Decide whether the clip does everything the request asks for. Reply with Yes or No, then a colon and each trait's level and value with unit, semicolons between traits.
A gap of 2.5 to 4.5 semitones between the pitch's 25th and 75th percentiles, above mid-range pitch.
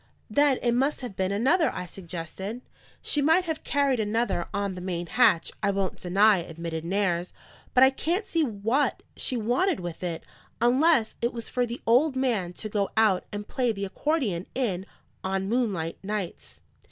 No: wide, 5.6 semitones; high, 215 Hz